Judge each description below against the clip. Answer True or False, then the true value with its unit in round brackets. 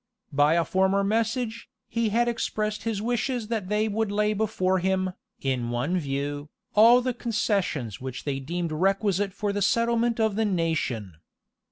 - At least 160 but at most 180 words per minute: True (165 wpm)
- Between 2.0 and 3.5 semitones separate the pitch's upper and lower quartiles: False (5.4 semitones)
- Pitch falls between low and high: False (200 Hz)